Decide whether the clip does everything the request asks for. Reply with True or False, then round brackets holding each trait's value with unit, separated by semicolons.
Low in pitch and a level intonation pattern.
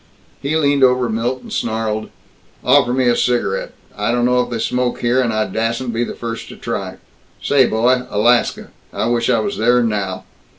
True (120 Hz; 1.9 semitones)